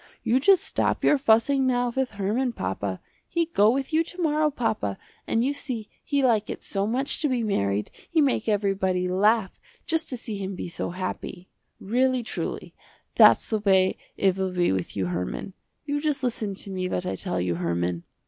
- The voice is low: No, high, 215 Hz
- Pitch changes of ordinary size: No, wide, 6.3 semitones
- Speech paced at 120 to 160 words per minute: No, average, 195 wpm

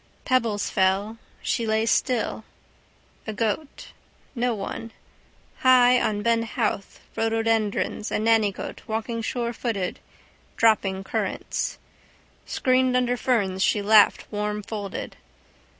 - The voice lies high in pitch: Yes, high, 225 Hz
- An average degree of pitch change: No, narrow, 2.3 semitones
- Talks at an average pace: No, slow, 100 wpm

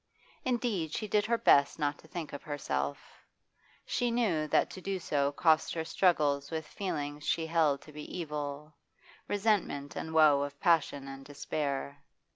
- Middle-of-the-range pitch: Yes, medium, 155 Hz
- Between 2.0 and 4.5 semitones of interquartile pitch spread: Yes, average, 3.4 semitones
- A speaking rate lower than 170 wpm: Yes, average, 160 wpm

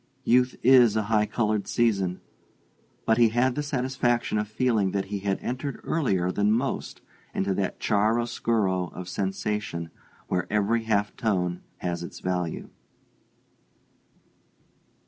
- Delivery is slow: Yes, slow, 125 wpm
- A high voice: No, low, 105 Hz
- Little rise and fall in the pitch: No, average, 3.7 semitones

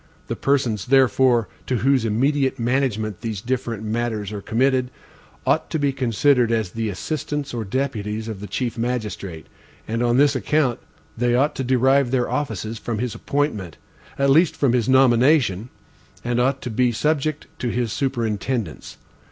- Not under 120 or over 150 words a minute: No, average, 160 wpm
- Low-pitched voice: Yes, low, 120 Hz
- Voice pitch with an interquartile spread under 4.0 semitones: Yes, average, 3.4 semitones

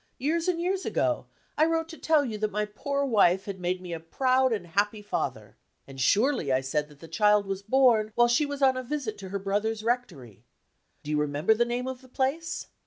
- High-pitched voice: Yes, high, 215 Hz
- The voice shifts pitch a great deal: Yes, wide, 6.2 semitones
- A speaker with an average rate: No, fast, 225 wpm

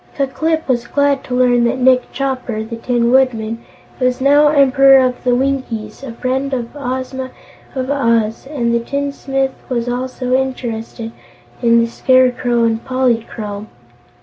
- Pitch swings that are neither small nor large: No, narrow, 2.3 semitones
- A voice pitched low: No, very high, 255 Hz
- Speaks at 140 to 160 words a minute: Yes, average, 150 wpm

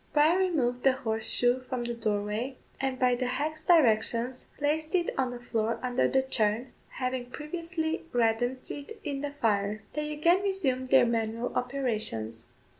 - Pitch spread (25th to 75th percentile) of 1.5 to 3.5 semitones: No, average, 4.2 semitones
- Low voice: No, very high, 255 Hz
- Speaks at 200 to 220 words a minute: No, average, 155 wpm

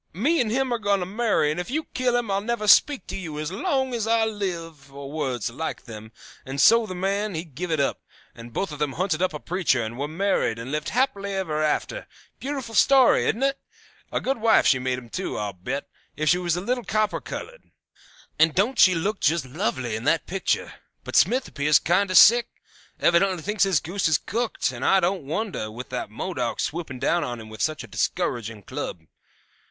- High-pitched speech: No, medium, 180 Hz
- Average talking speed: No, fast, 215 wpm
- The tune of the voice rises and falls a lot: Yes, wide, 7.3 semitones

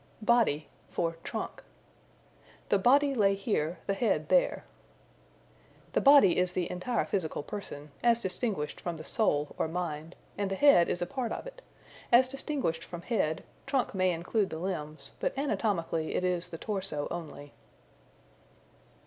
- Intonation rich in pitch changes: Yes, wide, 6.1 semitones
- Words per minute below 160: Yes, average, 150 wpm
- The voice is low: No, medium, 185 Hz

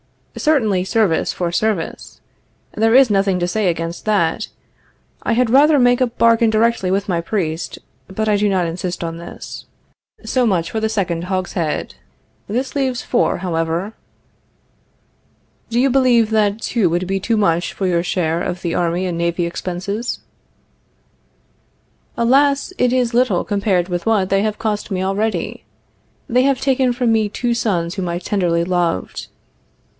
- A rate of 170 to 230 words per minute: No, average, 160 wpm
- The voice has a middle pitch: No, high, 200 Hz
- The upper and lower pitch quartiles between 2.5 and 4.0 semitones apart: No, average, 4.8 semitones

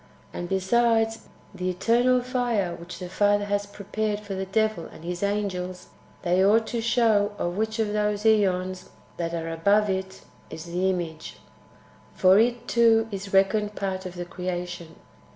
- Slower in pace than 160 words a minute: No, average, 170 wpm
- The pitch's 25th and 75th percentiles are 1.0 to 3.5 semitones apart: Yes, average, 3.2 semitones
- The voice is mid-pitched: No, high, 200 Hz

